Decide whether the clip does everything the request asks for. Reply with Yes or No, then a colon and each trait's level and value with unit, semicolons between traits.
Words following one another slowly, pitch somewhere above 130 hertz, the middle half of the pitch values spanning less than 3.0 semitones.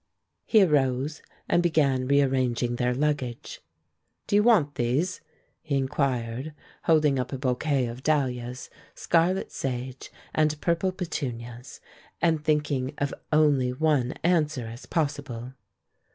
No: slow, 120 wpm; medium, 140 Hz; average, 3.7 semitones